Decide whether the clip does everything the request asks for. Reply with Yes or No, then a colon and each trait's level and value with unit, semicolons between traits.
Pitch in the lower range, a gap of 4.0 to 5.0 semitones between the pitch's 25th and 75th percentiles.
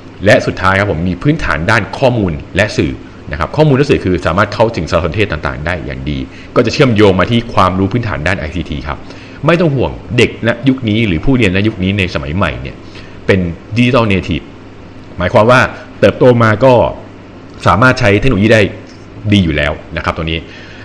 Yes: very low, 95 Hz; average, 4.5 semitones